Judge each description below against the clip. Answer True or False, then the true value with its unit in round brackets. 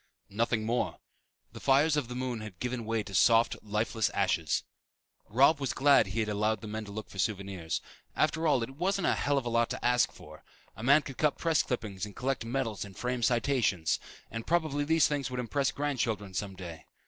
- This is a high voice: False (120 Hz)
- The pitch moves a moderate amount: True (4.5 semitones)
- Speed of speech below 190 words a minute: False (205 wpm)